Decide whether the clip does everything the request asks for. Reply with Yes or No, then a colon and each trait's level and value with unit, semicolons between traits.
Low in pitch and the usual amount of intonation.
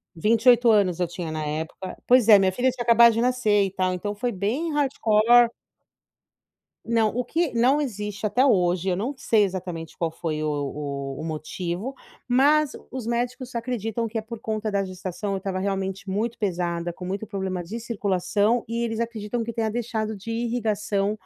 No: high, 210 Hz; average, 4.1 semitones